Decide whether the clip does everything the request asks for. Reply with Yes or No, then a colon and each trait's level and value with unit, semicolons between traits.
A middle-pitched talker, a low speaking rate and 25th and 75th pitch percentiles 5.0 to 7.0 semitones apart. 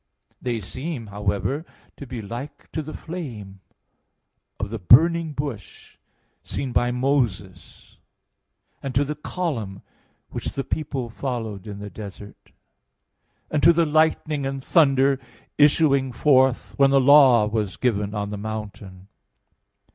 No: low, 125 Hz; slow, 130 wpm; wide, 5.6 semitones